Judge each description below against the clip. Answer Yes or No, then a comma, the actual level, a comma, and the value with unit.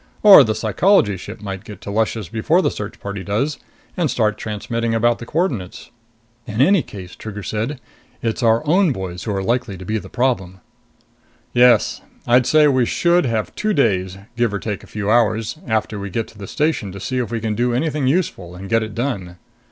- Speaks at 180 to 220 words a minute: Yes, fast, 205 wpm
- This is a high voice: No, low, 115 Hz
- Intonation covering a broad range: No, average, 4.1 semitones